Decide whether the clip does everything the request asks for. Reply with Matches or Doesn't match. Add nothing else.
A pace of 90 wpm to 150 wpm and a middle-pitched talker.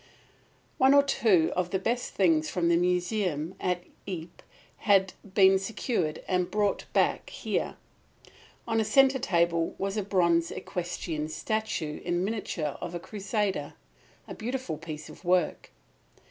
Matches